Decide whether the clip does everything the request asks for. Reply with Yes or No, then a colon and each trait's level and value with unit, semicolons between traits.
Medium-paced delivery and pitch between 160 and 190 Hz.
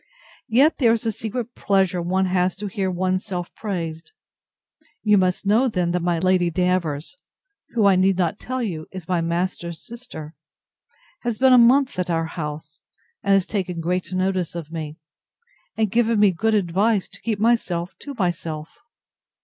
Yes: average, 170 wpm; medium, 185 Hz